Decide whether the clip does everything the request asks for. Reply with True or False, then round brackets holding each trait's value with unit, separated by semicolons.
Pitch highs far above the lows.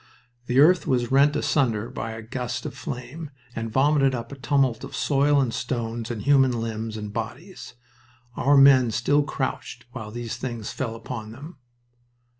False (3.3 semitones)